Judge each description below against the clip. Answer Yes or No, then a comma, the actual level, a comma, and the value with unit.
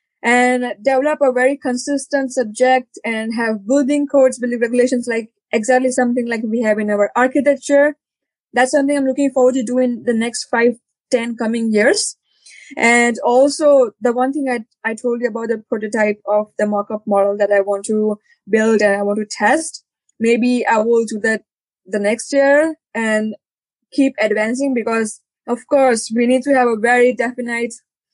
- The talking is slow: No, average, 175 wpm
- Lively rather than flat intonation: No, average, 2.7 semitones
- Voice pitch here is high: Yes, high, 240 Hz